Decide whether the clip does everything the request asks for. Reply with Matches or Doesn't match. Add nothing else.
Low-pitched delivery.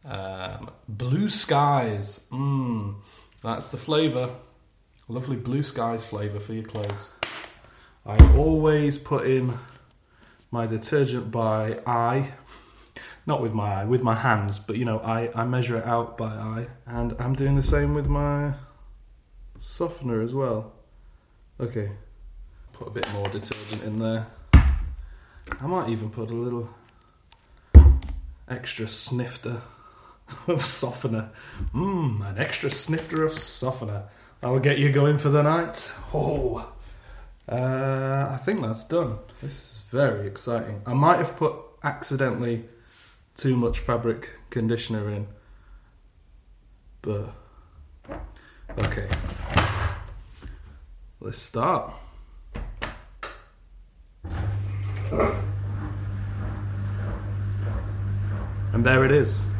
Matches